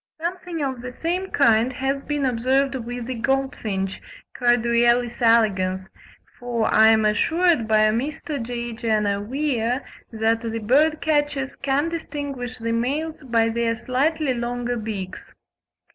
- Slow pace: Yes, slow, 130 wpm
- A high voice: Yes, high, 245 Hz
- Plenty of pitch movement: No, average, 3.6 semitones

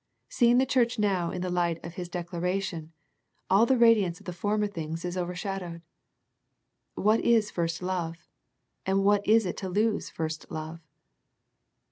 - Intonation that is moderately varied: Yes, average, 3.4 semitones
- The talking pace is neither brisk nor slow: Yes, average, 165 wpm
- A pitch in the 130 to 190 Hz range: Yes, medium, 185 Hz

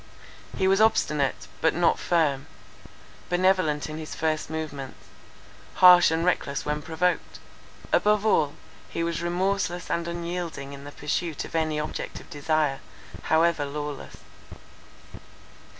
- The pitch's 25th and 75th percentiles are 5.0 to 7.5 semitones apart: No, average, 3.0 semitones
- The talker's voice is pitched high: No, medium, 160 Hz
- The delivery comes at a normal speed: No, slow, 125 wpm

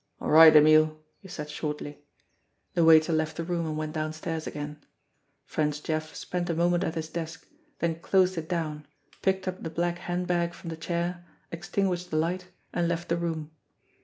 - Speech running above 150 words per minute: Yes, average, 185 wpm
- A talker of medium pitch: Yes, medium, 165 Hz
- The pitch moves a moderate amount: No, narrow, 2.0 semitones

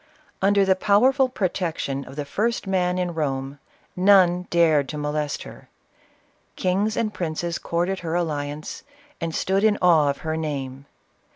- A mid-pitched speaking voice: Yes, medium, 170 Hz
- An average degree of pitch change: Yes, average, 4.3 semitones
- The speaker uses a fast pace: No, average, 155 wpm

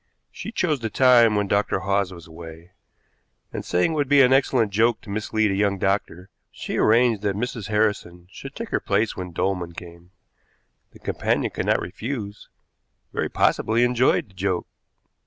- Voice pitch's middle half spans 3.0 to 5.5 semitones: Yes, average, 4.3 semitones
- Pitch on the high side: No, low, 105 Hz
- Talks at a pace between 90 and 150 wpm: No, average, 175 wpm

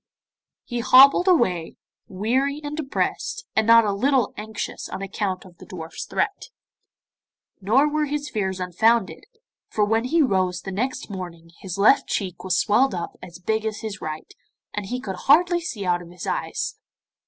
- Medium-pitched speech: No, high, 210 Hz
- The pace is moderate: Yes, average, 165 wpm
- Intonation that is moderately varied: No, wide, 6.1 semitones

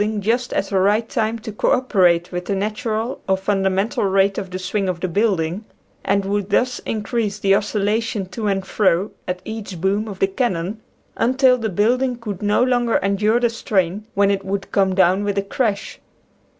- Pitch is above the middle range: Yes, high, 200 Hz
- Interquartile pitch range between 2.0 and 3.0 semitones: Yes, narrow, 2.5 semitones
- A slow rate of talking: No, average, 195 wpm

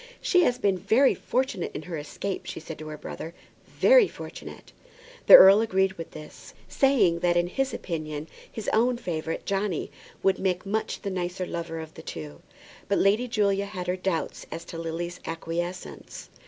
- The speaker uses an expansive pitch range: No, average, 3.7 semitones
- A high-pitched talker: No, medium, 180 Hz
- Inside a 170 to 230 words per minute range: Yes, average, 175 wpm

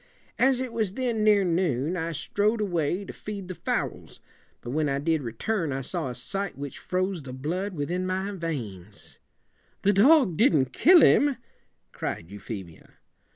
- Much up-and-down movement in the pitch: Yes, wide, 6.8 semitones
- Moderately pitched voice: Yes, medium, 180 Hz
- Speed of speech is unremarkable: Yes, average, 170 wpm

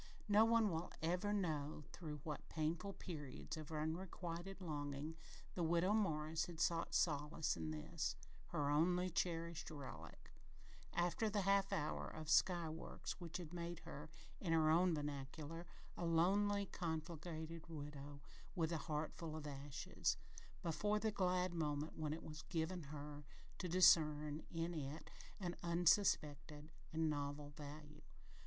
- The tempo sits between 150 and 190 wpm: No, average, 140 wpm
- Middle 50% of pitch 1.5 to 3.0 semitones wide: Yes, average, 2.7 semitones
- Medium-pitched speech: Yes, medium, 160 Hz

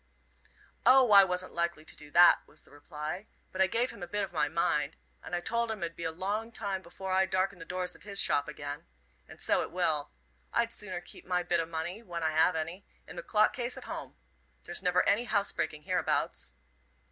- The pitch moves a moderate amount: Yes, average, 3.8 semitones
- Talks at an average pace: No, fast, 225 wpm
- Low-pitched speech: No, medium, 180 Hz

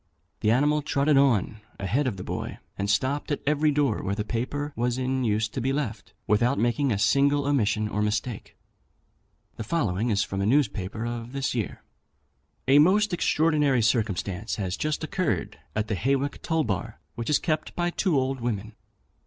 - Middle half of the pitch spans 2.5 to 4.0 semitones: No, average, 5.2 semitones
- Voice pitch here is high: No, low, 125 Hz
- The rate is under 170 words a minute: No, average, 180 wpm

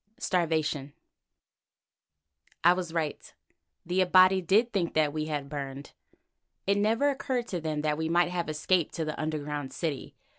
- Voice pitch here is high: No, medium, 165 Hz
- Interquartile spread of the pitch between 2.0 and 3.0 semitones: No, average, 3.5 semitones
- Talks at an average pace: Yes, average, 155 wpm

